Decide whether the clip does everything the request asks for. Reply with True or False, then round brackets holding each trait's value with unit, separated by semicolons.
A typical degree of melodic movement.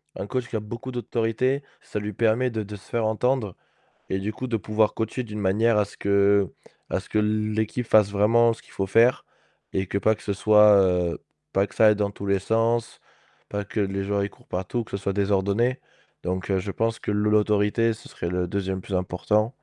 False (2.3 semitones)